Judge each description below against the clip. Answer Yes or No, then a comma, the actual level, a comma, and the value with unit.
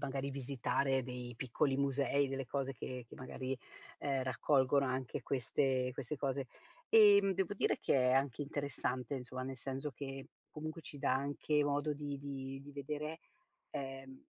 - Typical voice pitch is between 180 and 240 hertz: No, low, 135 Hz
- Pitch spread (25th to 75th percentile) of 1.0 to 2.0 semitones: Yes, narrow, 1.6 semitones